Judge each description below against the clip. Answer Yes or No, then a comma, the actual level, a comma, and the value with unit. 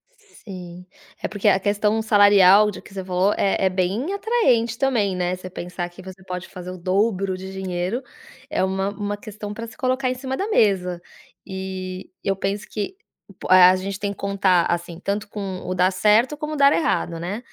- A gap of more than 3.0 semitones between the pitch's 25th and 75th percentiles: No, narrow, 2.6 semitones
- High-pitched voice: Yes, high, 195 Hz